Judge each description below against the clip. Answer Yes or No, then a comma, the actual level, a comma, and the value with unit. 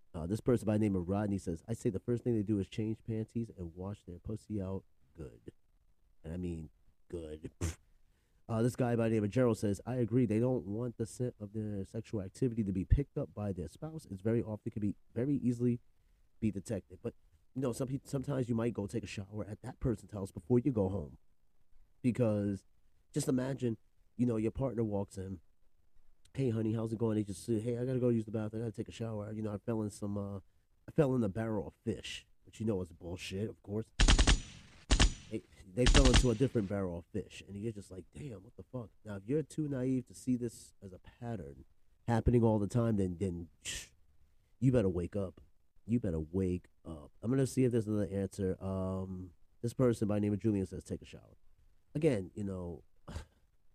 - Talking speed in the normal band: No, fast, 225 wpm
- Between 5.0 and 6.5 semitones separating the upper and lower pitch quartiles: No, average, 4.1 semitones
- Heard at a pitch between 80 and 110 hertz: Yes, low, 105 Hz